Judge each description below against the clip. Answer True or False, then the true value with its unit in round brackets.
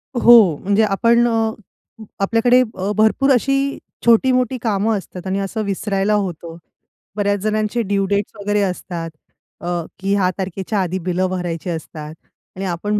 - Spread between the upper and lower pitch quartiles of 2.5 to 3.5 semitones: True (3.1 semitones)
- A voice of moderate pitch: False (200 Hz)